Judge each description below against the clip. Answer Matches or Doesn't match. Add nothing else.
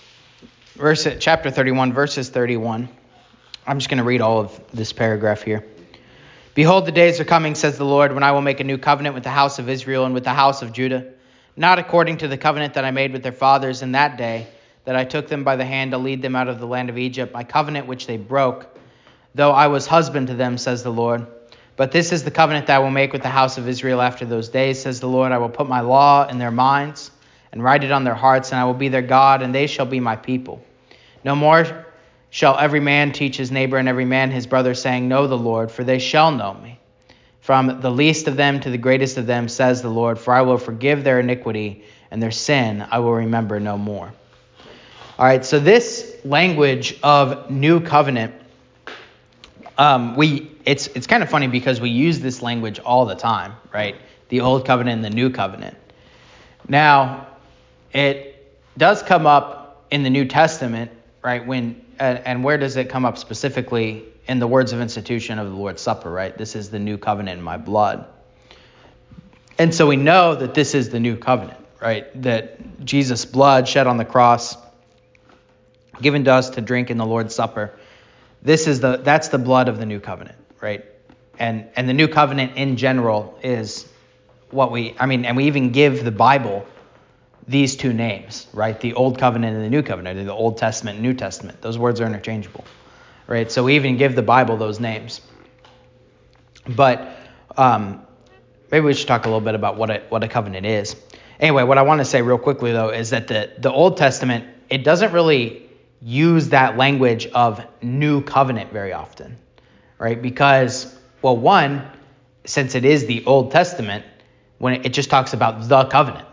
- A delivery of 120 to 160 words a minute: Doesn't match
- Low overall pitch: Matches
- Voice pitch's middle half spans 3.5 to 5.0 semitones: Doesn't match